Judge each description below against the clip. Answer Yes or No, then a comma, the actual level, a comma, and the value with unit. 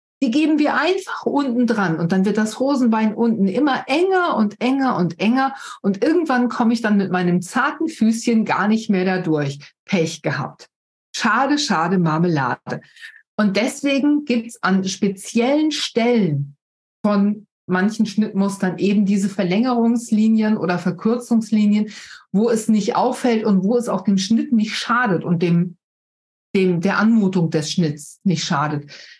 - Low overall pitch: No, high, 215 Hz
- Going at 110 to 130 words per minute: No, average, 150 wpm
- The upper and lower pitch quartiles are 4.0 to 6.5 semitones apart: Yes, average, 4.5 semitones